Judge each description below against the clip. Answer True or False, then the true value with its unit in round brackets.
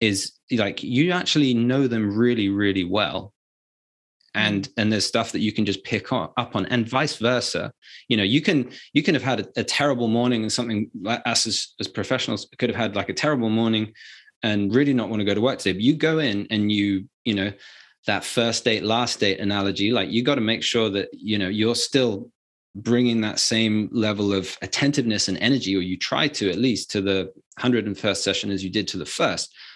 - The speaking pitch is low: True (110 Hz)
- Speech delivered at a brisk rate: True (215 wpm)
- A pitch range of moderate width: True (3.2 semitones)